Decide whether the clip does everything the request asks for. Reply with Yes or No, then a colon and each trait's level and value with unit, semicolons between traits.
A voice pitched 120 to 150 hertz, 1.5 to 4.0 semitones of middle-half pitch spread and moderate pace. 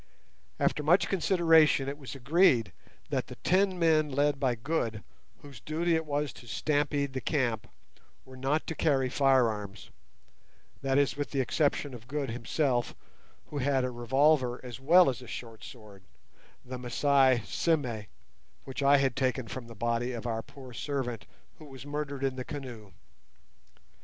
Yes: low, 135 Hz; average, 3.3 semitones; average, 155 wpm